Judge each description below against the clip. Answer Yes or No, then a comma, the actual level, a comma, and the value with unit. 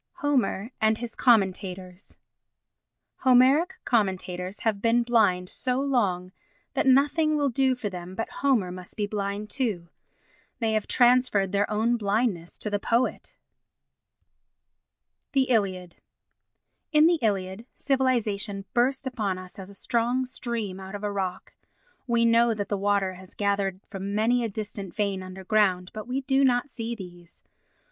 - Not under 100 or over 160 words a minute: Yes, average, 145 wpm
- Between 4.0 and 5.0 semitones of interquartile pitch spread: Yes, average, 4.3 semitones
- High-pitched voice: Yes, high, 215 Hz